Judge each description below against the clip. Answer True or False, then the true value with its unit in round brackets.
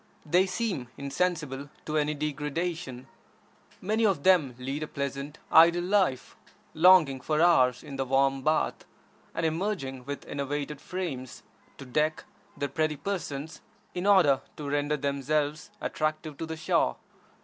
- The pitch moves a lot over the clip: False (3.7 semitones)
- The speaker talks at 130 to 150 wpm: True (140 wpm)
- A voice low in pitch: False (150 Hz)